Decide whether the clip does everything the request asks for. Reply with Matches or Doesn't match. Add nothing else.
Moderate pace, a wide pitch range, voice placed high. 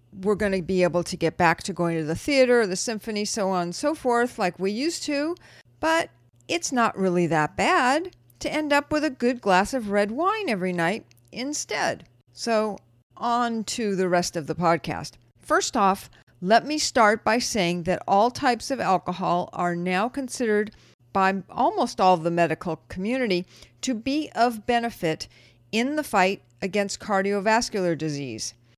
Matches